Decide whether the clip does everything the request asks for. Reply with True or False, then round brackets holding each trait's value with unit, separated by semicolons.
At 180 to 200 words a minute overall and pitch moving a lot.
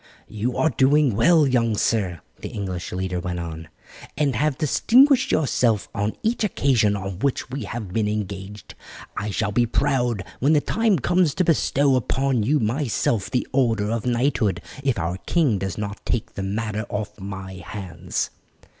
False (165 wpm; 5.7 semitones)